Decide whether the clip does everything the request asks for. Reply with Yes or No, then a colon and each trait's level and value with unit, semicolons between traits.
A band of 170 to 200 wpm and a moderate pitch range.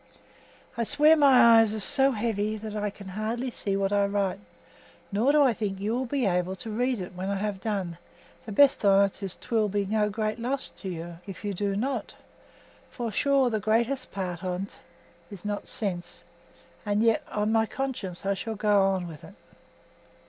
Yes: average, 190 wpm; average, 3.0 semitones